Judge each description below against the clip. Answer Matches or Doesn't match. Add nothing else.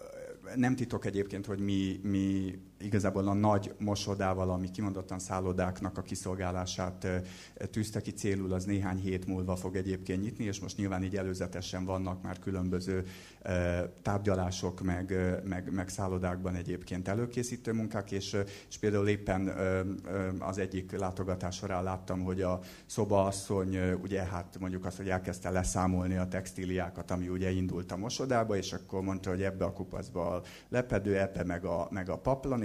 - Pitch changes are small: Matches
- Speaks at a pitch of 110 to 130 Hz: Doesn't match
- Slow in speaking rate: Doesn't match